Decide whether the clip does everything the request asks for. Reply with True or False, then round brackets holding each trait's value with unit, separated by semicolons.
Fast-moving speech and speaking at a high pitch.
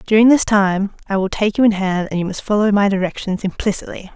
True (230 wpm; 200 Hz)